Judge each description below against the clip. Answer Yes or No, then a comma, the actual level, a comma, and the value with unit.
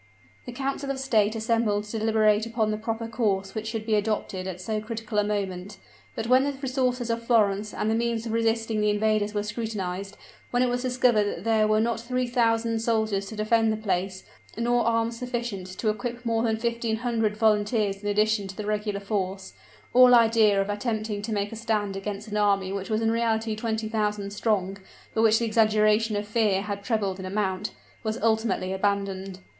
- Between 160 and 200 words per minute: Yes, average, 195 wpm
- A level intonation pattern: Yes, narrow, 1.9 semitones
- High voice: Yes, high, 220 Hz